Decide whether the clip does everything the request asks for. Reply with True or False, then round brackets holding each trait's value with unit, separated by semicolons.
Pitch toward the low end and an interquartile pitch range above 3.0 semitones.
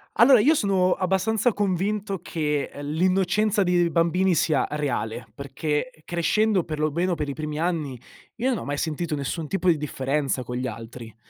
False (170 Hz; 4.8 semitones)